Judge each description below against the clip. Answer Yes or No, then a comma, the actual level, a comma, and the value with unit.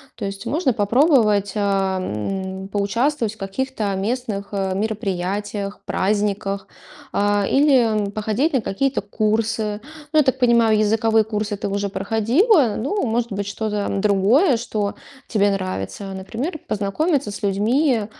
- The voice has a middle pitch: No, high, 210 Hz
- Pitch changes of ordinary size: Yes, average, 3.2 semitones